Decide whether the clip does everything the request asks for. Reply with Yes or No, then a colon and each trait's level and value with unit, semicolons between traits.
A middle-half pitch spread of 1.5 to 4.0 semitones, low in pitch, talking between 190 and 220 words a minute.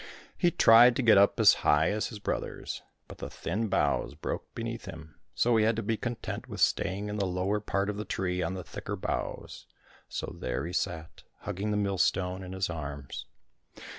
Yes: average, 3.0 semitones; low, 100 Hz; average, 195 wpm